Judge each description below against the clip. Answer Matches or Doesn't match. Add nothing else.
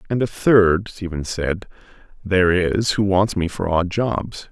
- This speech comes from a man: Matches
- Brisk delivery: Doesn't match